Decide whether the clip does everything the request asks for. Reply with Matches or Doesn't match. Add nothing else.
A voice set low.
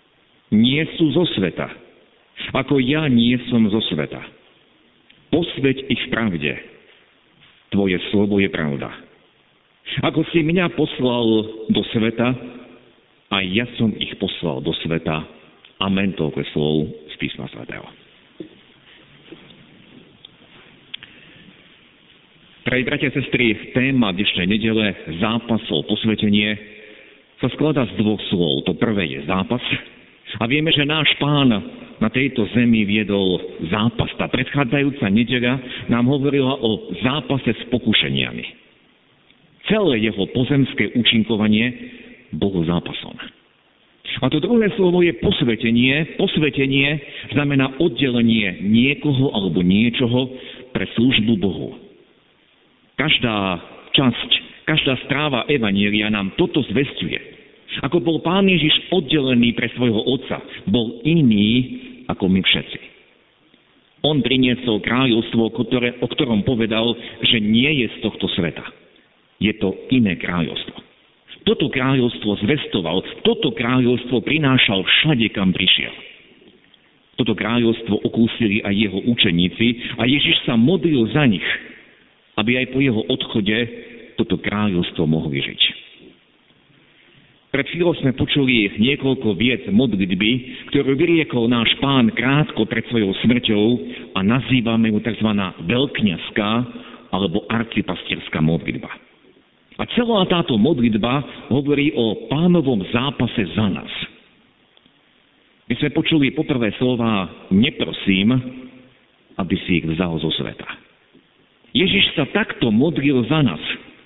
Matches